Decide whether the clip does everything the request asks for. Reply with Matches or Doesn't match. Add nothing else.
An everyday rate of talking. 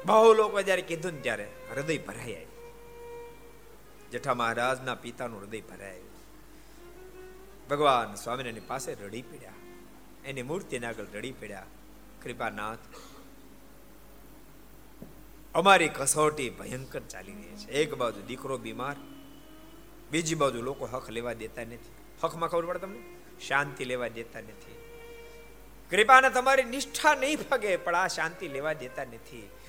Matches